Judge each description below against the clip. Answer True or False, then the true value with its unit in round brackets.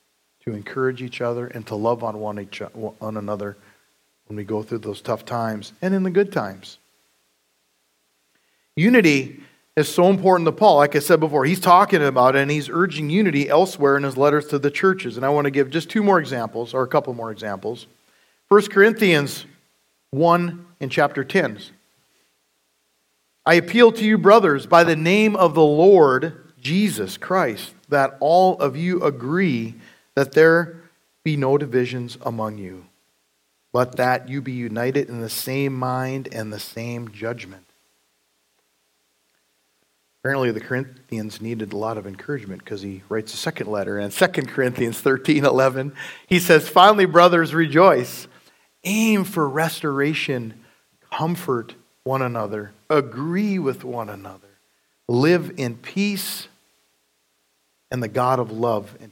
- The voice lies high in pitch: False (130 Hz)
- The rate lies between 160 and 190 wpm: False (150 wpm)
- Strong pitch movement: True (7.3 semitones)